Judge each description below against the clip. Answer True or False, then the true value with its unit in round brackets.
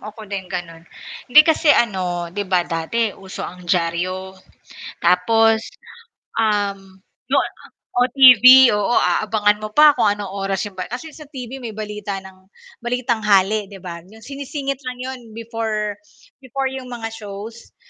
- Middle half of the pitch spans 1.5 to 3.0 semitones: False (4.2 semitones)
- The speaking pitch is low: False (215 Hz)